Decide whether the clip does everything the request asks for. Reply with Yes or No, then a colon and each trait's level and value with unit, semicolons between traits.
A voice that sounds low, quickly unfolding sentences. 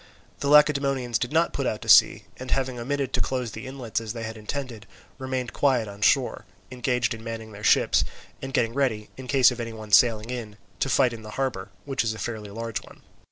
Yes: low, 120 Hz; fast, 225 wpm